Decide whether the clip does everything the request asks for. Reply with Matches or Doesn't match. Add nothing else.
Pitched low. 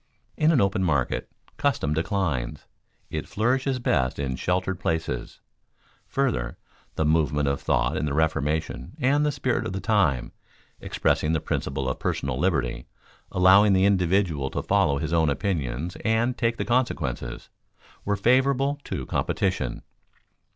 Matches